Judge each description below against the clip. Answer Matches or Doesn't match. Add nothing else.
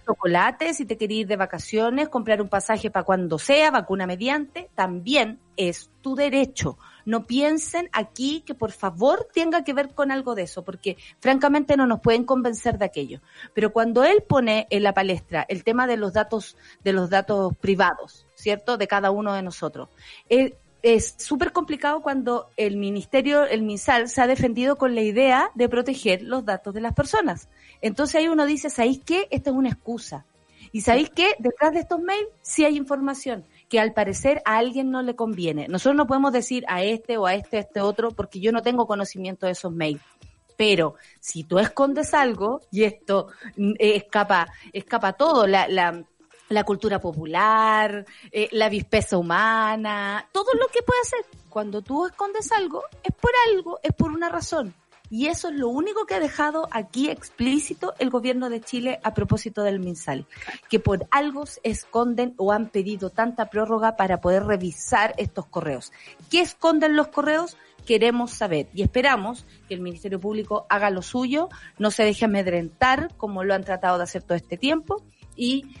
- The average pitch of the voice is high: Matches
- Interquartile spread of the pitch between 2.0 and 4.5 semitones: Doesn't match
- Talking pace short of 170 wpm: Doesn't match